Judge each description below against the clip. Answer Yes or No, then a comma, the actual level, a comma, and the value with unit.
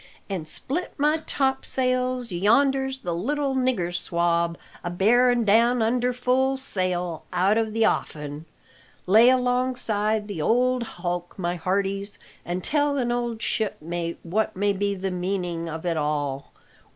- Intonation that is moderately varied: No, wide, 6.2 semitones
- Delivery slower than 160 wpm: Yes, average, 140 wpm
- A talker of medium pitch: No, high, 210 Hz